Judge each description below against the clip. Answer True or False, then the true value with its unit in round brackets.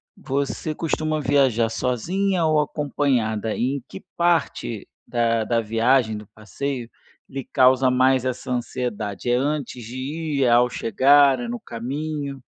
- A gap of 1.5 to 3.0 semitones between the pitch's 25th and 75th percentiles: False (3.6 semitones)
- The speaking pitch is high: False (130 Hz)